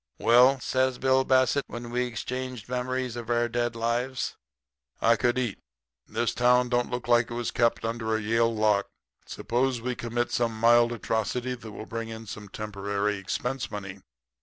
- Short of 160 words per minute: No, average, 170 wpm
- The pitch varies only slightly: Yes, narrow, 1.8 semitones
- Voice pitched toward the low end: Yes, low, 120 Hz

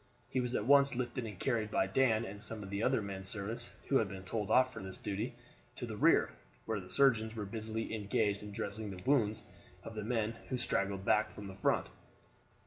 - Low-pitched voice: Yes, low, 110 Hz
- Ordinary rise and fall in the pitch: Yes, average, 3.0 semitones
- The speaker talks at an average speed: No, fast, 220 wpm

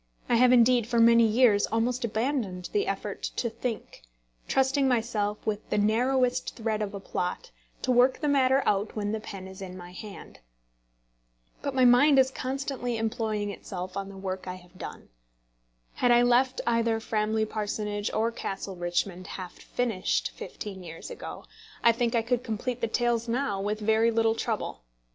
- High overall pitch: Yes, high, 225 Hz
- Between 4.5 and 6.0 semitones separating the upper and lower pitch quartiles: No, average, 3.3 semitones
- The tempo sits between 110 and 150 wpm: No, average, 170 wpm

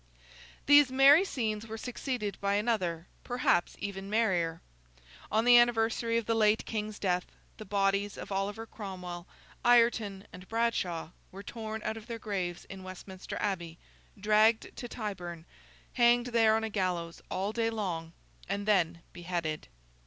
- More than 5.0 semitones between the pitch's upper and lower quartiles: No, average, 3.6 semitones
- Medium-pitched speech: No, high, 210 Hz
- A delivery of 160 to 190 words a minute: No, average, 145 wpm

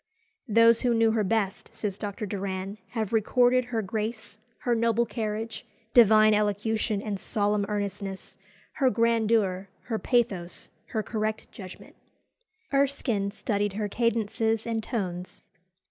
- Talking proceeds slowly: Yes, slow, 125 wpm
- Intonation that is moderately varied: No, narrow, 2.2 semitones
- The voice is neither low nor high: No, high, 215 Hz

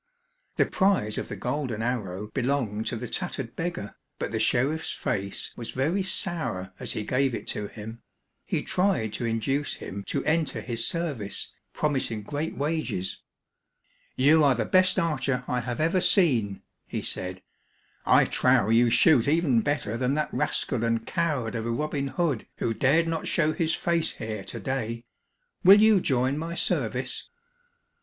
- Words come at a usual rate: Yes, average, 160 wpm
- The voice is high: No, low, 130 Hz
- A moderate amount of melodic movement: No, wide, 5.9 semitones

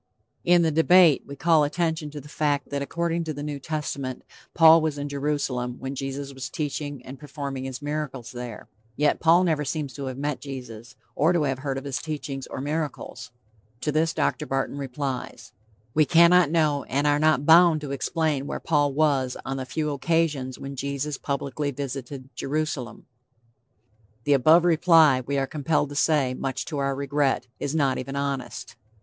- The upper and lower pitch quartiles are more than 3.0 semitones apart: No, narrow, 2.5 semitones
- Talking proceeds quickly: No, average, 180 wpm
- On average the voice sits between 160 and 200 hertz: No, medium, 145 Hz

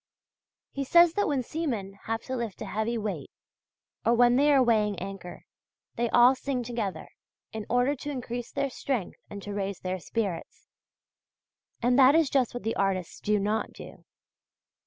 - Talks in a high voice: Yes, high, 235 Hz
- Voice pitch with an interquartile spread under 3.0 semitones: No, average, 4.3 semitones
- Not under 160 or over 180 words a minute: Yes, average, 170 wpm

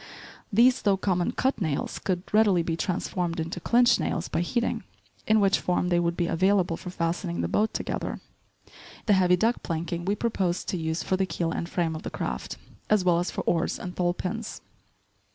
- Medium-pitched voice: Yes, medium, 180 Hz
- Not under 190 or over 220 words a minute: Yes, average, 195 wpm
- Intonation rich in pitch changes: No, average, 2.9 semitones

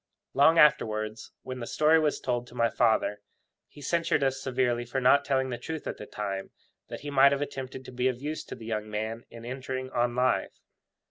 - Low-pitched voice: Yes, low, 130 Hz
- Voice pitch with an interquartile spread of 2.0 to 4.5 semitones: Yes, average, 2.9 semitones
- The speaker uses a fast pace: Yes, fast, 210 wpm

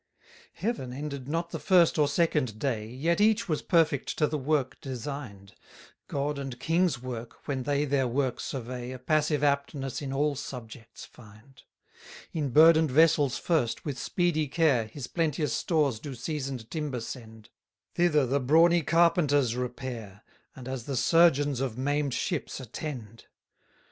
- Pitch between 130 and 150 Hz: Yes, medium, 140 Hz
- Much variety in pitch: No, average, 3.7 semitones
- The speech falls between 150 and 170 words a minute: Yes, average, 155 wpm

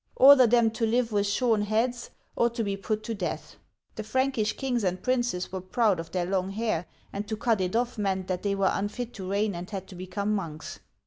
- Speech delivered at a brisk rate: Yes, fast, 220 wpm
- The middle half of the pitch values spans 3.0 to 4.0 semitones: Yes, average, 3.7 semitones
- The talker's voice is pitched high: Yes, high, 210 Hz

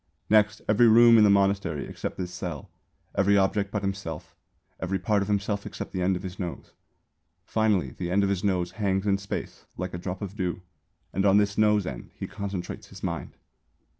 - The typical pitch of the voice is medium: No, low, 100 Hz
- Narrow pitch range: Yes, narrow, 2.0 semitones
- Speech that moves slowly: No, average, 195 wpm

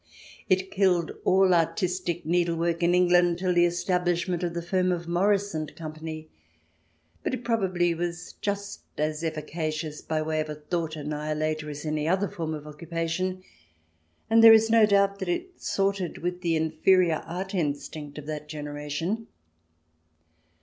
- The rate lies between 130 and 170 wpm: Yes, average, 150 wpm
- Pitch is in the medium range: Yes, medium, 170 Hz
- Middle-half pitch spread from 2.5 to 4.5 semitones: Yes, average, 3.1 semitones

